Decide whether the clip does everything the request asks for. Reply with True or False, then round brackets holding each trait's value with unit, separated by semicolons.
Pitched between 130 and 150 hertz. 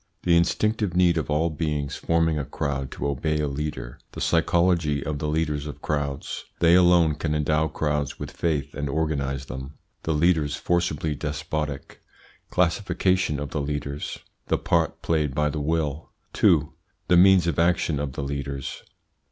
False (75 Hz)